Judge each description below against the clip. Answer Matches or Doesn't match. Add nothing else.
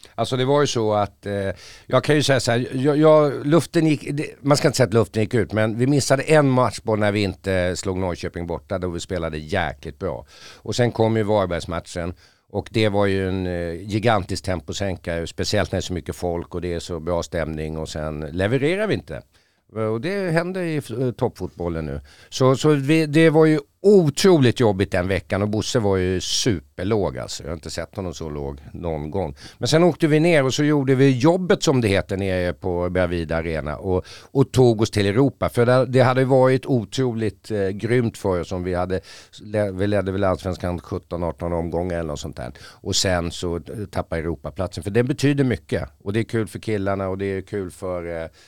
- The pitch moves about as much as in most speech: Doesn't match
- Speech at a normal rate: Doesn't match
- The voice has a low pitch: Matches